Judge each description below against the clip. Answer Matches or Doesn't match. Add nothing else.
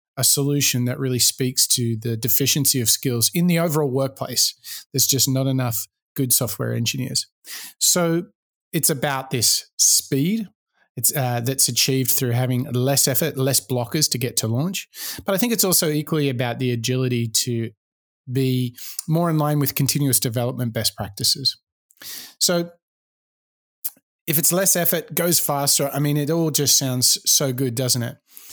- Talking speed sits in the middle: Matches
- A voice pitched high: Doesn't match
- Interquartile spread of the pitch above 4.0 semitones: Doesn't match